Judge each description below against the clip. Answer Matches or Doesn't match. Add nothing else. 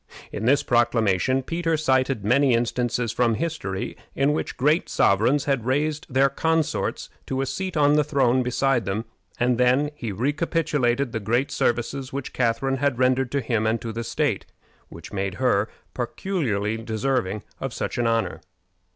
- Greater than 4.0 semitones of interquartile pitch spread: Doesn't match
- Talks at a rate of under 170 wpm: Matches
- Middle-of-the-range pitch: Doesn't match